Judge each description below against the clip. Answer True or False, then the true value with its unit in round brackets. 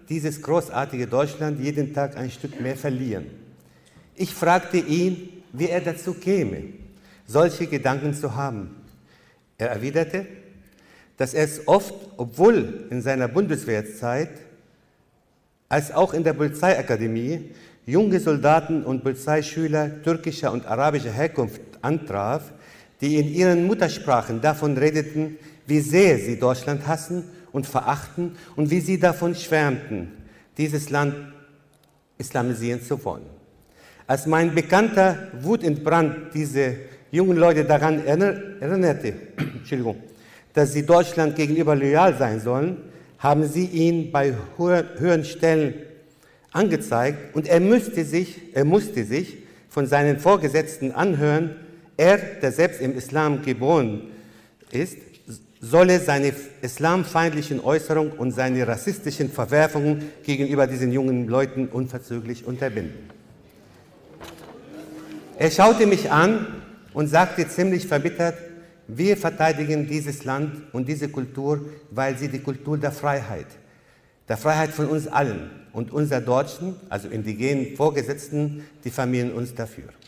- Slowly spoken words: True (120 wpm)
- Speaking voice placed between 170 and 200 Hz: False (150 Hz)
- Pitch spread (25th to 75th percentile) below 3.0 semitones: False (4.0 semitones)